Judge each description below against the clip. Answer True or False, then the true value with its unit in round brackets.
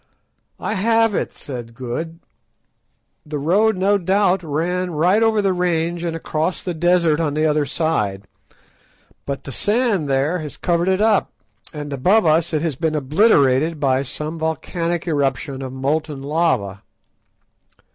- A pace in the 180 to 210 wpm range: False (145 wpm)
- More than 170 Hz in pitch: False (160 Hz)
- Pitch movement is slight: False (4.1 semitones)